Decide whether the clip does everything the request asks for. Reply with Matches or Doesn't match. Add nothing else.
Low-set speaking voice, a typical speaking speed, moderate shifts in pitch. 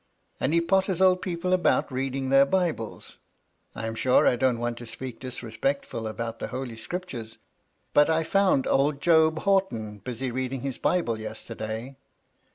Doesn't match